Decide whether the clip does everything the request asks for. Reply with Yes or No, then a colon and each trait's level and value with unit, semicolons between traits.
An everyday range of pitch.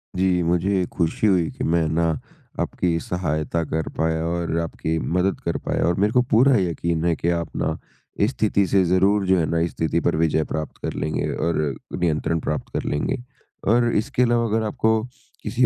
Yes: average, 3.6 semitones